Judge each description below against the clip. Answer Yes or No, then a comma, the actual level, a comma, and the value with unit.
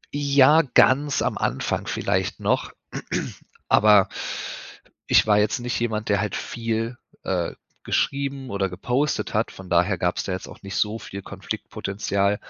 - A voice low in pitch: Yes, low, 105 Hz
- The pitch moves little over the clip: No, average, 4.1 semitones